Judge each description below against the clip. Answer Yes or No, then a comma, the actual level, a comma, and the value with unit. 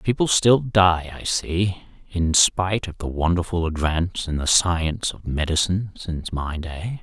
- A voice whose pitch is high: No, very low, 90 Hz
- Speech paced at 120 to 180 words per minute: Yes, average, 160 wpm